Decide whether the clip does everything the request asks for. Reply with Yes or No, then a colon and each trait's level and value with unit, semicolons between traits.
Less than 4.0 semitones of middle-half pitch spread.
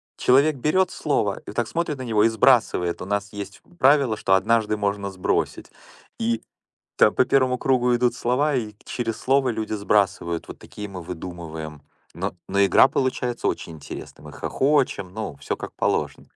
No: average, 4.6 semitones